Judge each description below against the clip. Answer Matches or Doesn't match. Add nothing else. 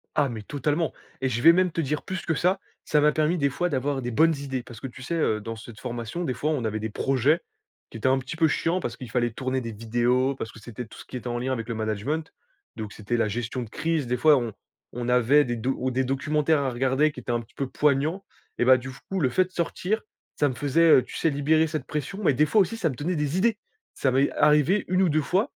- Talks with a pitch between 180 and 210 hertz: Doesn't match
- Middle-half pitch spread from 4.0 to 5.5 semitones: Matches